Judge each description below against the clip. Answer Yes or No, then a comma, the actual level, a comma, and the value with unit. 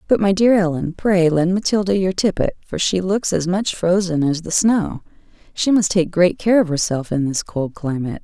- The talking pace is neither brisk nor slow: No, fast, 210 wpm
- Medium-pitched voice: Yes, medium, 180 Hz